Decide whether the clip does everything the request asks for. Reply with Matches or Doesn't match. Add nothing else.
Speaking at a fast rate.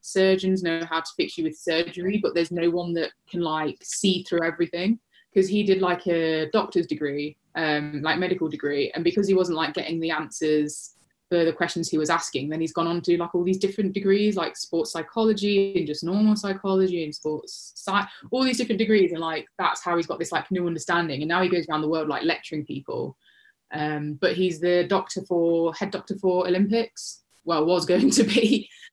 Matches